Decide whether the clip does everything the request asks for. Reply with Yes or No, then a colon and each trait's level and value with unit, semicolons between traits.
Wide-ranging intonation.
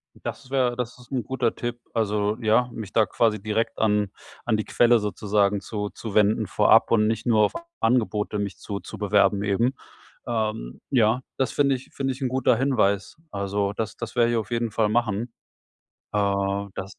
No: average, 2.7 semitones